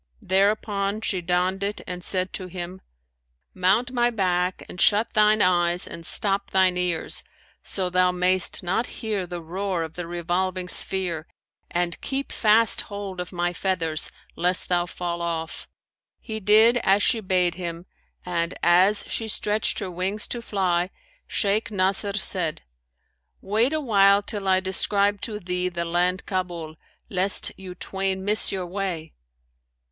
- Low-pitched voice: No, medium, 185 Hz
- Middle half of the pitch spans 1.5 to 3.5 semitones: Yes, narrow, 2.4 semitones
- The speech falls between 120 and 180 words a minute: Yes, average, 150 wpm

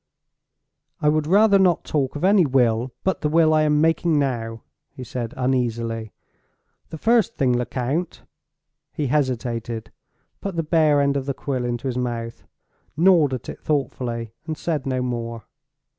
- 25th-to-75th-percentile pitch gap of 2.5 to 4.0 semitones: No, average, 4.5 semitones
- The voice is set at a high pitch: No, low, 135 Hz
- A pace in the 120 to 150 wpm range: Yes, average, 145 wpm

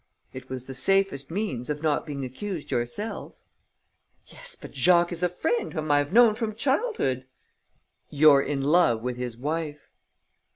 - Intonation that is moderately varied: No, wide, 6.8 semitones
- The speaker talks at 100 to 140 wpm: No, average, 160 wpm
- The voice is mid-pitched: Yes, medium, 150 Hz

